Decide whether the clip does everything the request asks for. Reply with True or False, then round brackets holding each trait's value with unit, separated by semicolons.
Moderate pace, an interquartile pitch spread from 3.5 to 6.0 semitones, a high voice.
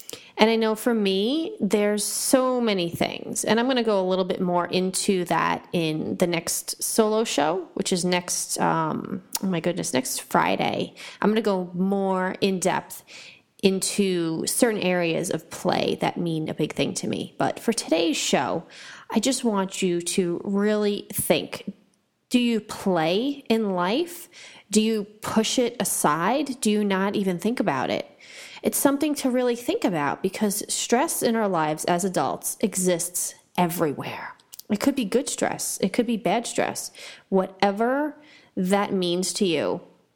True (165 wpm; 4.2 semitones; 205 Hz)